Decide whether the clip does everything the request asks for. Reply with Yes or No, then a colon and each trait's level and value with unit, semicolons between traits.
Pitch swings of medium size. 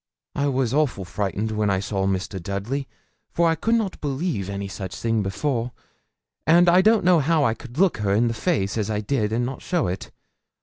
No: wide, 7.4 semitones